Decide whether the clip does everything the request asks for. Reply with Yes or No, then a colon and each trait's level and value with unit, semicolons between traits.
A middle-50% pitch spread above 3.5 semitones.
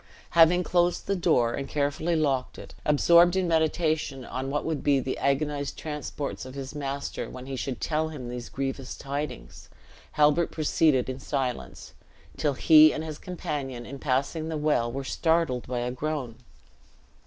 No: average, 3.2 semitones